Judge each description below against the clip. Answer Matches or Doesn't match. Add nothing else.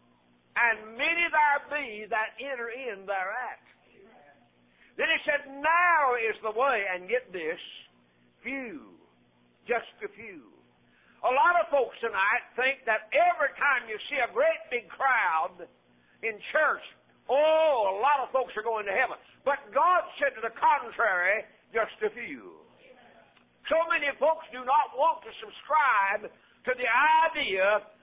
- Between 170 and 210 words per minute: Doesn't match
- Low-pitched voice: Doesn't match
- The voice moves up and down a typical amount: Doesn't match